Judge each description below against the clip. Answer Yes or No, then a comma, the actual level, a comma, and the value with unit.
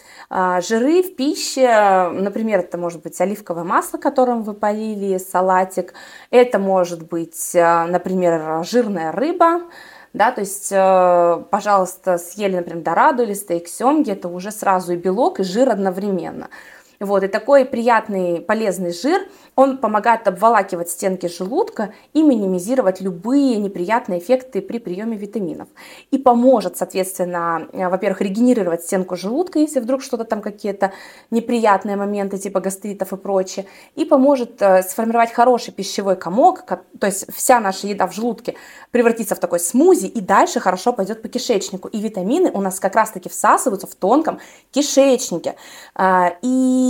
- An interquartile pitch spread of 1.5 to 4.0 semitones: No, average, 5.0 semitones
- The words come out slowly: No, average, 140 wpm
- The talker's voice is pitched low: No, high, 200 Hz